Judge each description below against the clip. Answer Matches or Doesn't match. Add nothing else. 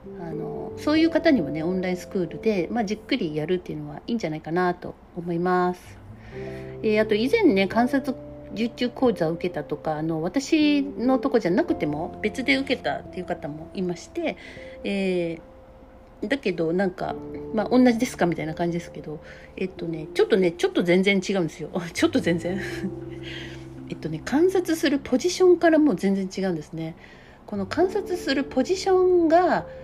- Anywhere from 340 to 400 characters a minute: Matches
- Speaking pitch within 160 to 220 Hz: Matches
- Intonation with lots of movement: Matches